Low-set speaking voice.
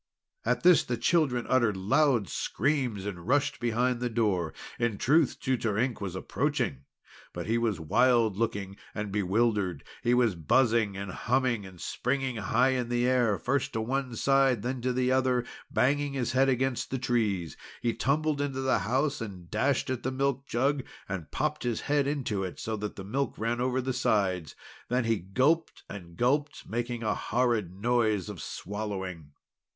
Yes: low, 120 Hz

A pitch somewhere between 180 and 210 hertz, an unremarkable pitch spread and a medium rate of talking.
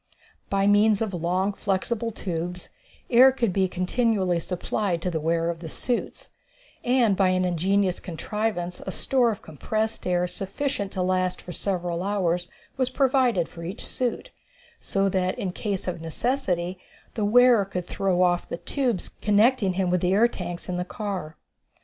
Yes: high, 190 Hz; average, 3.5 semitones; average, 165 wpm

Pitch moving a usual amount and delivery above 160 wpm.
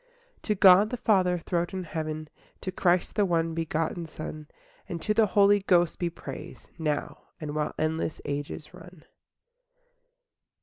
No: average, 3.1 semitones; average, 155 wpm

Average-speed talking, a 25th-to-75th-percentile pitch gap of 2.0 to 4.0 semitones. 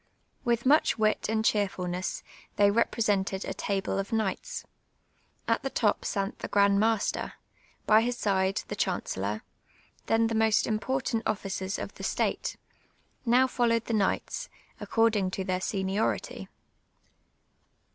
No: slow, 130 wpm; average, 2.8 semitones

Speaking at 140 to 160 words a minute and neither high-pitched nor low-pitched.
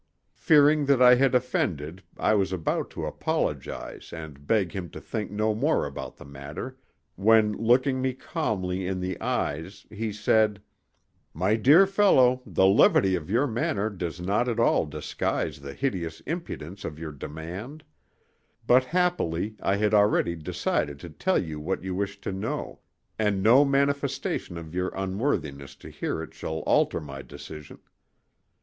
No: average, 155 wpm; low, 100 Hz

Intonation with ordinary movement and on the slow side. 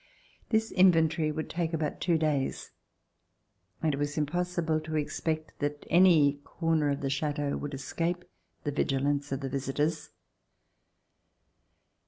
No: narrow, 2.3 semitones; slow, 130 wpm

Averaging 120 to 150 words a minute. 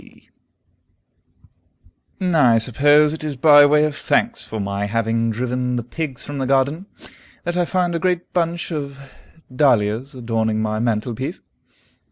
Yes: average, 145 wpm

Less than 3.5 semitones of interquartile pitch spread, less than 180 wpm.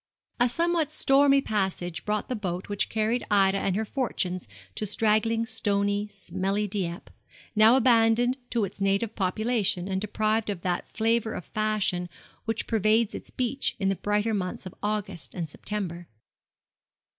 Yes: average, 2.7 semitones; average, 150 wpm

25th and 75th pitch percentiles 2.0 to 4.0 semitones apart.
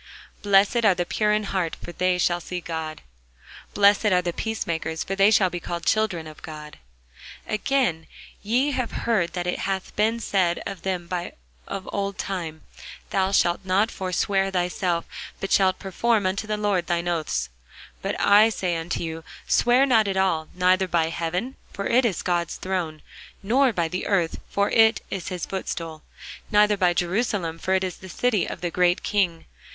Yes: average, 3.1 semitones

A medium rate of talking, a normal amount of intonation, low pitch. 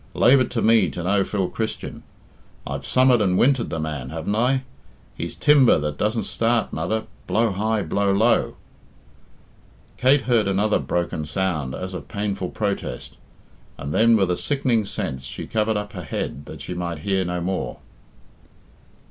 Yes: average, 165 wpm; average, 4.7 semitones; low, 100 Hz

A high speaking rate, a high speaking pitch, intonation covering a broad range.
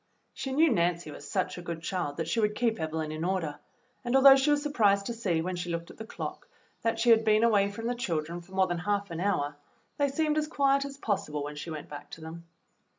Yes: fast, 250 wpm; high, 195 Hz; wide, 6.3 semitones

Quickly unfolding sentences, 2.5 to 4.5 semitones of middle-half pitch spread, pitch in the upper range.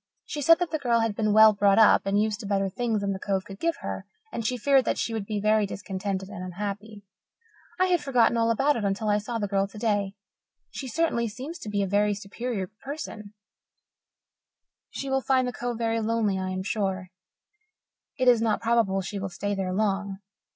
Yes: fast, 210 wpm; average, 3.0 semitones; high, 215 Hz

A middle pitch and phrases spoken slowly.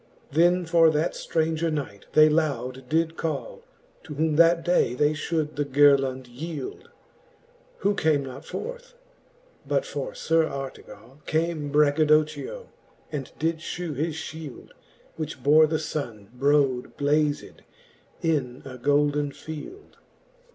Yes: medium, 155 Hz; slow, 125 wpm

